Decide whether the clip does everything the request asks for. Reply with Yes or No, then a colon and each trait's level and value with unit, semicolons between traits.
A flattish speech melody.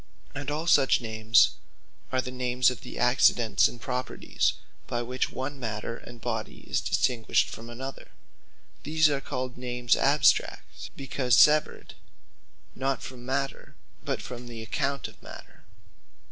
Yes: narrow, 2.2 semitones